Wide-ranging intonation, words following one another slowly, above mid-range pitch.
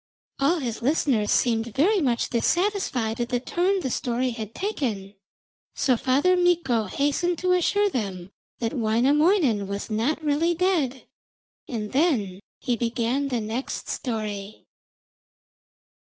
Yes: wide, 6.6 semitones; slow, 125 wpm; very high, 255 Hz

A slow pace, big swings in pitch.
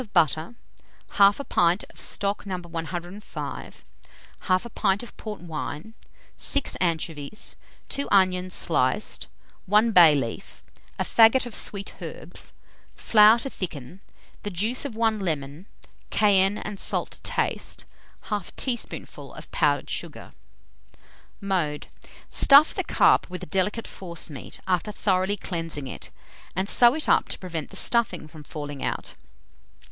No: slow, 130 wpm; average, 4.4 semitones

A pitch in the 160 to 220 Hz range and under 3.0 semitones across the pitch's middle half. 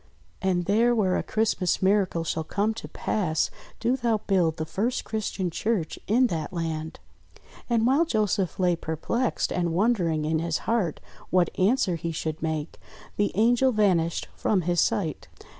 No: medium, 185 Hz; average, 5.1 semitones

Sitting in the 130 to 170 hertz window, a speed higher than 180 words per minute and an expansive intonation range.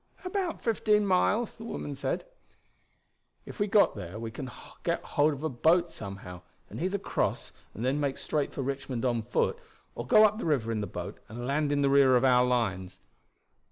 Yes: medium, 140 Hz; average, 195 wpm; wide, 7.7 semitones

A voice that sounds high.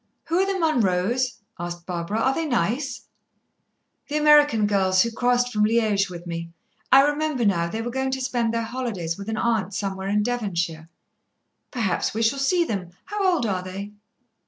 Yes: high, 225 Hz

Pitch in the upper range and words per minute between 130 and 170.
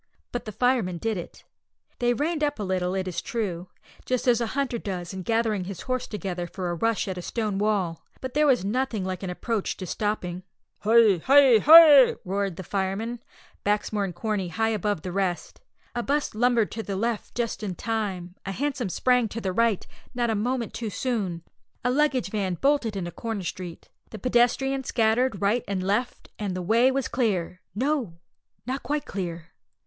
No: high, 215 Hz; average, 190 wpm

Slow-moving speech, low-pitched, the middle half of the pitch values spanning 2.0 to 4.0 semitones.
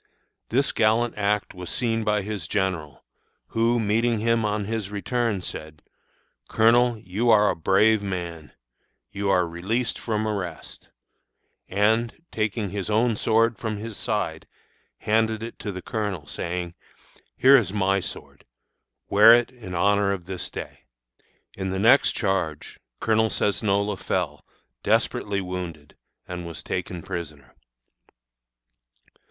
Yes: slow, 130 wpm; low, 105 Hz; average, 3.4 semitones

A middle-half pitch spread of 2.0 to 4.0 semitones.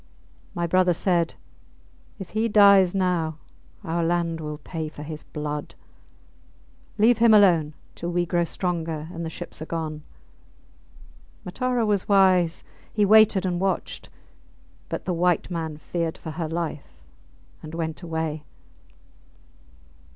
Yes: average, 2.9 semitones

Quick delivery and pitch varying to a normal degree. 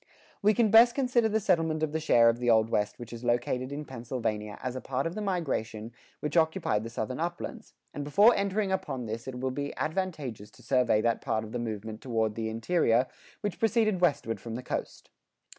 No: fast, 210 wpm; wide, 7.6 semitones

